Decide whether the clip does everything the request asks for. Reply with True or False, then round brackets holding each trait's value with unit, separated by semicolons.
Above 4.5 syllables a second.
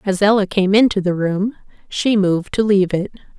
True (5.5 syllables/s)